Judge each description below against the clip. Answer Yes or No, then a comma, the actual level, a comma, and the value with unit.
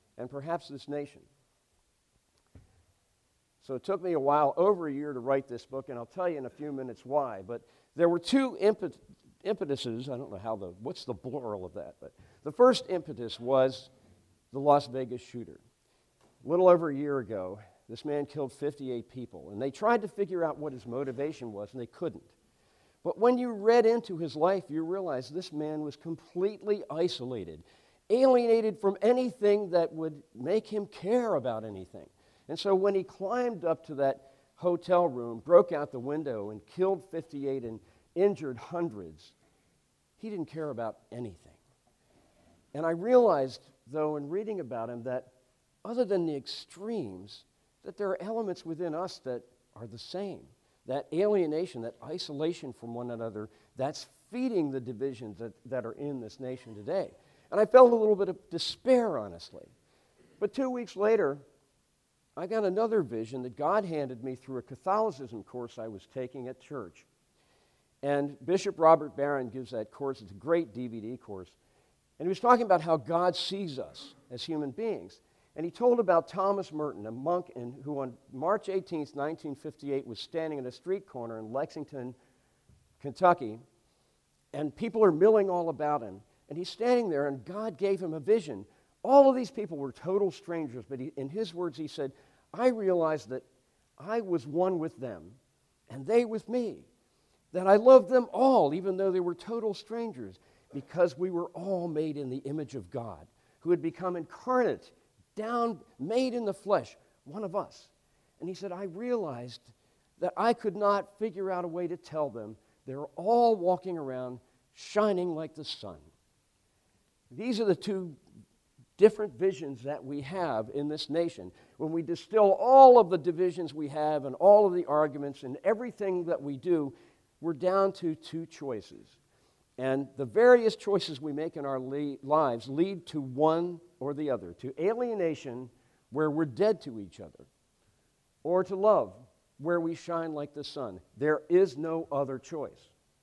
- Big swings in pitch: Yes, wide, 6.6 semitones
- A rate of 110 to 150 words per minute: No, average, 175 wpm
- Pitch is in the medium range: Yes, medium, 155 Hz